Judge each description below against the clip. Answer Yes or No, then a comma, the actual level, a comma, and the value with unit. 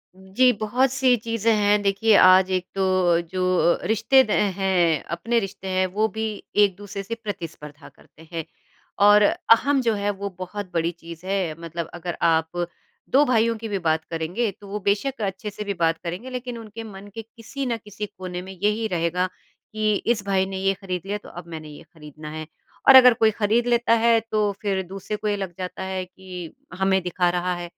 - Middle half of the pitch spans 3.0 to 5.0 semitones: Yes, average, 3.4 semitones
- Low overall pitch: No, high, 195 Hz